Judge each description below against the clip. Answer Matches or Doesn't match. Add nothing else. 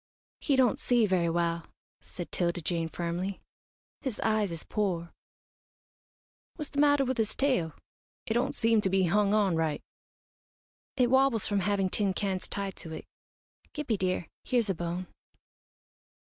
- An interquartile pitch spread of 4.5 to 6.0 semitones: Matches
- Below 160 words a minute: Matches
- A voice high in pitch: Matches